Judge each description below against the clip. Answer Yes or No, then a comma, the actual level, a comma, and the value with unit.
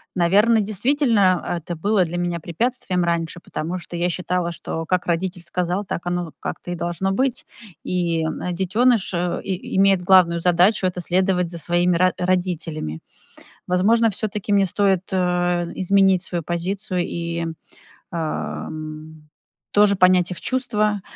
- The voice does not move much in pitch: Yes, narrow, 2.2 semitones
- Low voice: No, medium, 180 Hz